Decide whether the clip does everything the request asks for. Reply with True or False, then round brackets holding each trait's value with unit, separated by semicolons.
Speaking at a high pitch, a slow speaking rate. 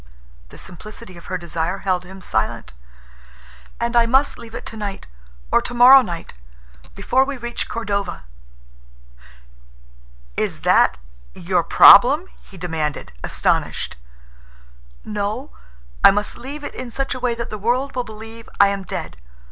True (210 Hz; 130 wpm)